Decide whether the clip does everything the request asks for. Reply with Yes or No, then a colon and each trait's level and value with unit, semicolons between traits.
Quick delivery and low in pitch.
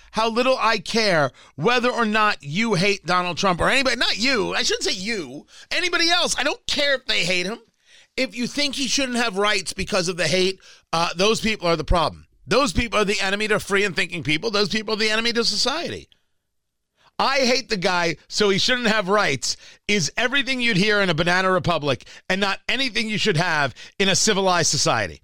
No: fast, 210 wpm; high, 205 Hz